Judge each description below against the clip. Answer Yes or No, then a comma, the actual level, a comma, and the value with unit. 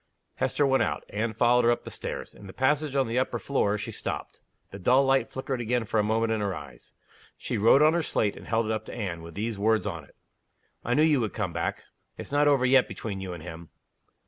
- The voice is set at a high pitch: No, low, 115 Hz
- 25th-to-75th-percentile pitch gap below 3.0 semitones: No, average, 4.6 semitones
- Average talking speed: No, fast, 250 wpm